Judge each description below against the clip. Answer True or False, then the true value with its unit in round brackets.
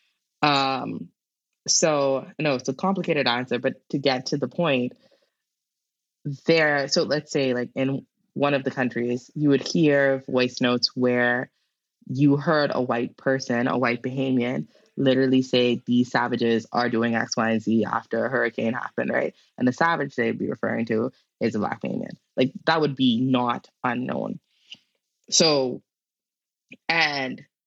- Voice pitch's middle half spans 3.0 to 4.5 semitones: False (2.6 semitones)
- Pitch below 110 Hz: False (130 Hz)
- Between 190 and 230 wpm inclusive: False (155 wpm)